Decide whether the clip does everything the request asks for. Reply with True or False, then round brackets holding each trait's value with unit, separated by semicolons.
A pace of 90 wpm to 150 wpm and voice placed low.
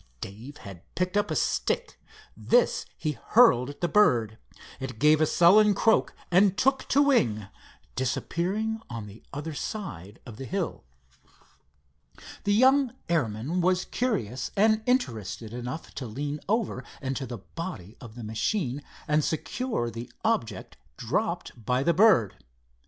False (140 wpm; 150 Hz)